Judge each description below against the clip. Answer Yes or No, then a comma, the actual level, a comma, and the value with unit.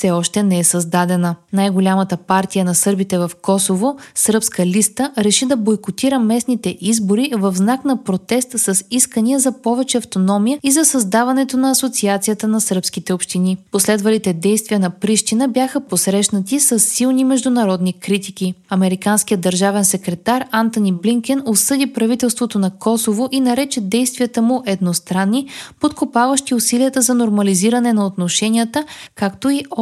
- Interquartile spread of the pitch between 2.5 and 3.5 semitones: No, average, 4.6 semitones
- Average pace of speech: Yes, average, 135 wpm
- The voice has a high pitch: Yes, high, 215 Hz